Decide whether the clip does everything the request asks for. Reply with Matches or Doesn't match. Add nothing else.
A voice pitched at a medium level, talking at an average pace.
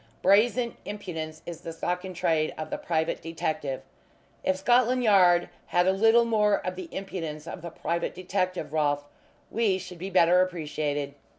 Matches